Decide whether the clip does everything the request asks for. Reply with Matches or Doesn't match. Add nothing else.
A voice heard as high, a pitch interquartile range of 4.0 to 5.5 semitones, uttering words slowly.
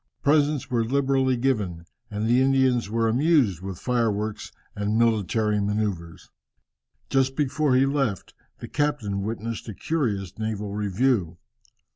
Doesn't match